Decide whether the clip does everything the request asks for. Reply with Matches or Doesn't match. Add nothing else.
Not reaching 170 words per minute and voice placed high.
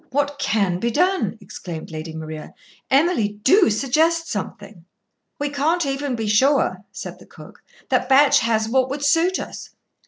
Matches